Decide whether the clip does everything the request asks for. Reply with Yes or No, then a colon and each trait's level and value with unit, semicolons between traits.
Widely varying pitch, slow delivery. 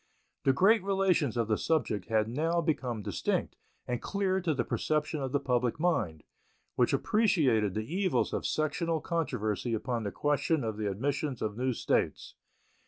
No: wide, 6.7 semitones; average, 165 wpm